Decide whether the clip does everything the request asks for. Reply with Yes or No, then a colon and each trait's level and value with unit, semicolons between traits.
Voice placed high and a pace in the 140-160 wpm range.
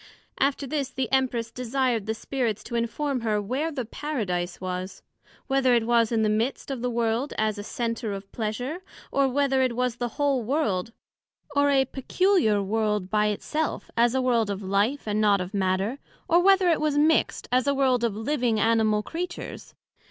No: high, 240 Hz; average, 190 wpm